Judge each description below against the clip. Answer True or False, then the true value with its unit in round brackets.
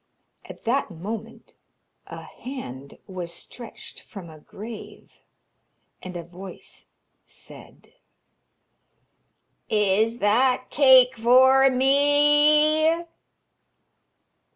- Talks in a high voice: True (235 Hz)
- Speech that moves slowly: True (80 wpm)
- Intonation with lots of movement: True (5.7 semitones)